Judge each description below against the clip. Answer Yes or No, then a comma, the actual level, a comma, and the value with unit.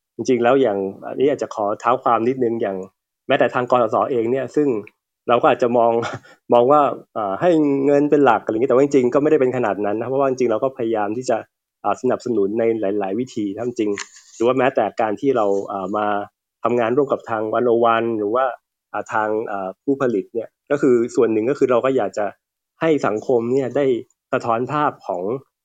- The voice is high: No, low, 115 Hz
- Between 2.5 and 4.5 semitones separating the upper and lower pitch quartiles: Yes, average, 4.2 semitones